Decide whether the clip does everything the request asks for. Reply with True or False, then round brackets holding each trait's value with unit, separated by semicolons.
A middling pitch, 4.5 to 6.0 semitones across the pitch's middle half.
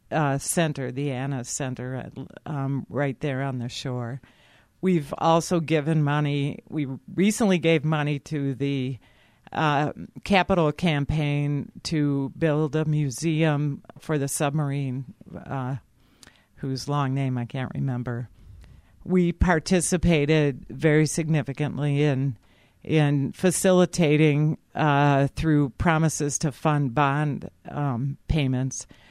False (145 Hz; 2.8 semitones)